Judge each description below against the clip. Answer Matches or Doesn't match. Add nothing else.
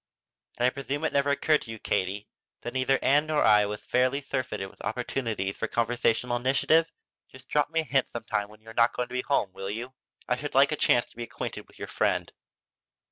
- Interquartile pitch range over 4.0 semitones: Doesn't match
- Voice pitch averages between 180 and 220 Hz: Doesn't match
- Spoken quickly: Matches